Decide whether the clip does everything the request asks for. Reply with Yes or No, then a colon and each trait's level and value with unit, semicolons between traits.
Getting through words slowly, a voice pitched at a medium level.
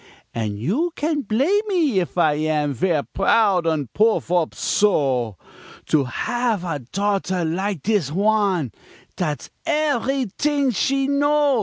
No: slow, 130 wpm; high, 200 Hz